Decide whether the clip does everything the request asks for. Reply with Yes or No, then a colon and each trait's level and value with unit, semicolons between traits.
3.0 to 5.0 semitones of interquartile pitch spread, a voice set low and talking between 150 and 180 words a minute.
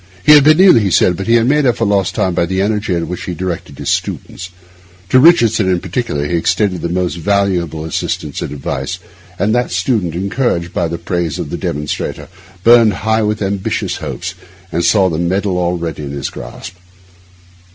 No: average, 4.1 semitones; very low, 95 Hz; average, 195 wpm